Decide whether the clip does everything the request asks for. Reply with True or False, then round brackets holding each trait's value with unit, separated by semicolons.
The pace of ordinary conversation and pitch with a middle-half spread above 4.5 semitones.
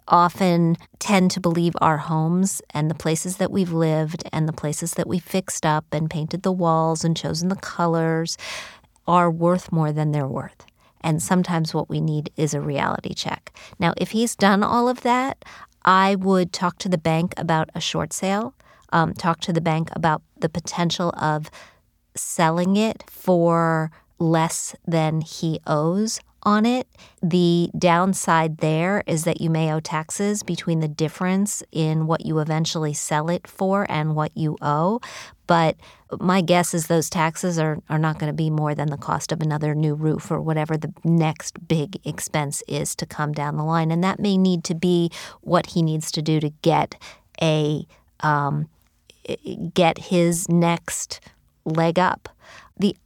False (175 wpm; 2.5 semitones)